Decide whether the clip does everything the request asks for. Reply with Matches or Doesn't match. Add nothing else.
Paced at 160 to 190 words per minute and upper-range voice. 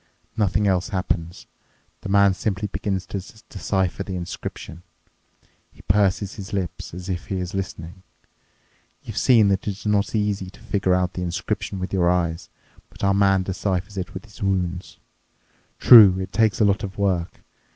Doesn't match